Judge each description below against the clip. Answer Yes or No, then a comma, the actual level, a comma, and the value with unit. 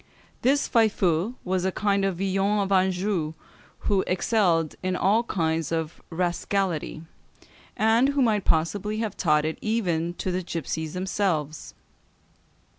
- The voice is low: No, medium, 185 Hz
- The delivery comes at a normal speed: No, slow, 130 wpm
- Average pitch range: Yes, average, 4.0 semitones